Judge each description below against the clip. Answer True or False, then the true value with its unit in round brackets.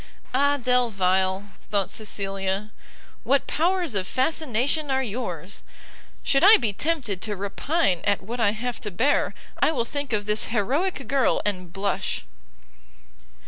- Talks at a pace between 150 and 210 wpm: False (140 wpm)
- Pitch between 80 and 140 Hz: False (225 Hz)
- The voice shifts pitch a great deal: True (5.8 semitones)